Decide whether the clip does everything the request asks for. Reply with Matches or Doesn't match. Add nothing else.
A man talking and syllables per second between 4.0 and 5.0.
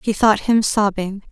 Doesn't match